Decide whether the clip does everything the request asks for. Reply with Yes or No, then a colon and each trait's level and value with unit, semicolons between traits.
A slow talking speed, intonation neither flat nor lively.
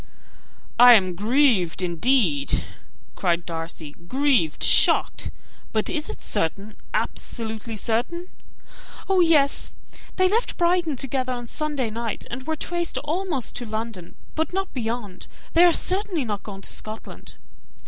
No: slow, 130 wpm; wide, 7.3 semitones